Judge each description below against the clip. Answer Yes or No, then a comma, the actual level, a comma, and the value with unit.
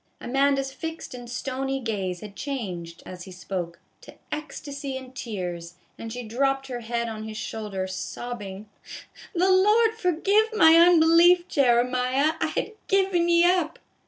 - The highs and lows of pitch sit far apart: Yes, wide, 7.4 semitones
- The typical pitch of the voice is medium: No, very high, 260 Hz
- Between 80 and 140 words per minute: No, average, 150 wpm